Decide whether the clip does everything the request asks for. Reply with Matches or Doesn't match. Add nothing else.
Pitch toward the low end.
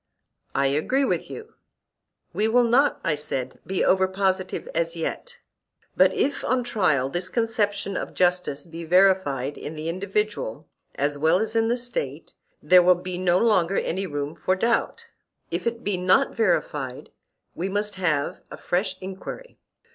Doesn't match